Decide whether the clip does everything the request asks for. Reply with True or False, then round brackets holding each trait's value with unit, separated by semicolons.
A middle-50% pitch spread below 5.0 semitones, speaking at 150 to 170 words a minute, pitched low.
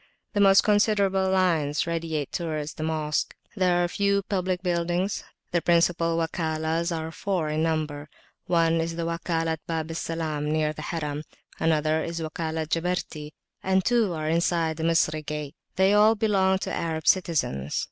False (2.6 semitones; 155 wpm; 165 Hz)